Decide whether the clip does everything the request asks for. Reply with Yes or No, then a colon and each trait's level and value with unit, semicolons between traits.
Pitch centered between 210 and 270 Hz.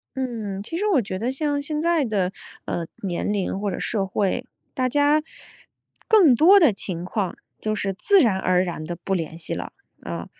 Yes: high, 215 Hz